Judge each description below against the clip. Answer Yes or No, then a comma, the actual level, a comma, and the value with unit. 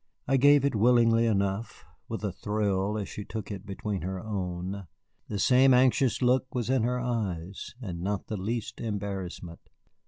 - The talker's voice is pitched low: Yes, low, 105 Hz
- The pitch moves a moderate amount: Yes, average, 4.0 semitones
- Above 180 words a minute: No, average, 165 wpm